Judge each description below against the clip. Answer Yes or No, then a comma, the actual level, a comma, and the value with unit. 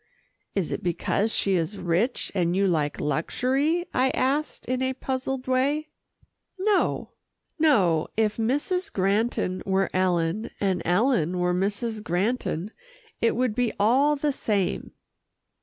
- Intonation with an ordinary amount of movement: No, wide, 6.2 semitones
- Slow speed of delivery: Yes, slow, 130 wpm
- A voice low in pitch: No, high, 215 Hz